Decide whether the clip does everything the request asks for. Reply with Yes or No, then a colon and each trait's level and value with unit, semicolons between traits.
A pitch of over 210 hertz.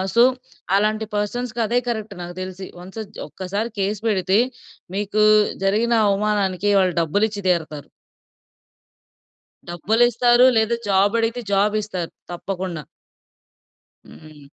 No: high, 205 Hz